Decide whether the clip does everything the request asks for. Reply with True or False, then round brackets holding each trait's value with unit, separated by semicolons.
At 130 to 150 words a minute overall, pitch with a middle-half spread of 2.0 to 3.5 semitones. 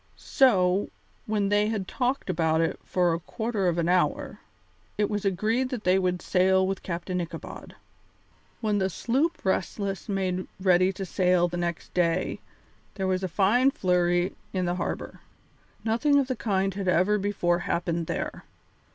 False (160 wpm; 2.8 semitones)